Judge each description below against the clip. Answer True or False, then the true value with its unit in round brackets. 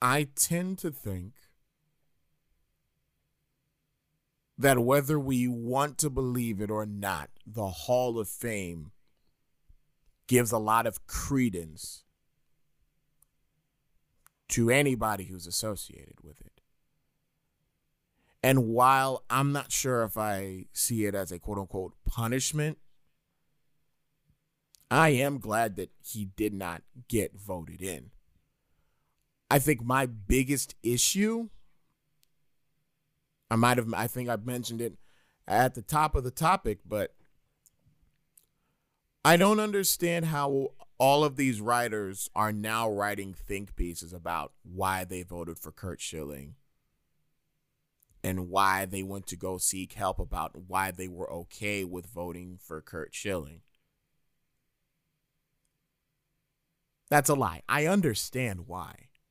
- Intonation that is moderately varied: False (7.2 semitones)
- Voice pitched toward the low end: True (120 Hz)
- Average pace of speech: False (115 wpm)